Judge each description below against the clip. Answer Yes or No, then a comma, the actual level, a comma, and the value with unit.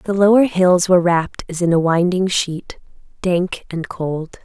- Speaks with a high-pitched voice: No, medium, 180 Hz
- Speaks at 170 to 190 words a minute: Yes, average, 175 wpm